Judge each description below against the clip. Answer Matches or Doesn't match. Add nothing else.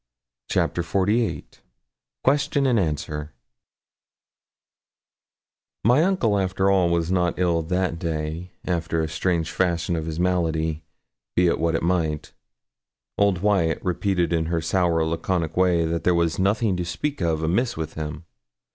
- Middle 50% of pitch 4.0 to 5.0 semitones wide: Doesn't match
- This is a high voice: Doesn't match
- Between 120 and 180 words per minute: Matches